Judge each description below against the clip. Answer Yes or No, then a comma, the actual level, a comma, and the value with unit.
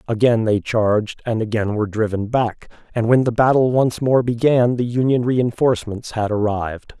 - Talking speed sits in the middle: Yes, average, 170 wpm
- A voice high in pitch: No, low, 115 Hz